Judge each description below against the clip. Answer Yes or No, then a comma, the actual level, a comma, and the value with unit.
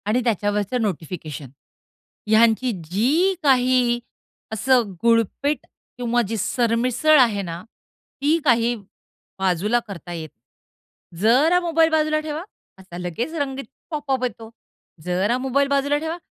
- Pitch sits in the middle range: No, high, 240 Hz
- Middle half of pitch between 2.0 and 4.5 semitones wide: No, wide, 5.5 semitones